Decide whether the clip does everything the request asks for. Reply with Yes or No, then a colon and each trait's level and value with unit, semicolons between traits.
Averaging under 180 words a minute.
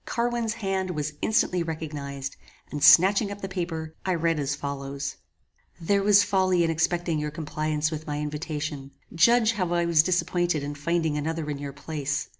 Yes: average, 170 wpm